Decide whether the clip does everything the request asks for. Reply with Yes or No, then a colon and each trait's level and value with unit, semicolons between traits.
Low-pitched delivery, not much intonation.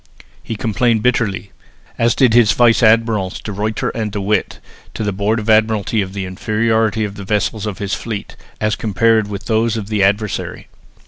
Yes: low, 110 Hz; narrow, 1.9 semitones